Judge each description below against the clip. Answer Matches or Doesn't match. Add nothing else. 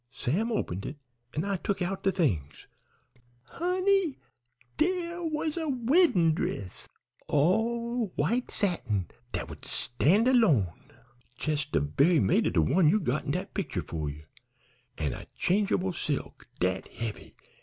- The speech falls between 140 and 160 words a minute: Matches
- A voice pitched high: Doesn't match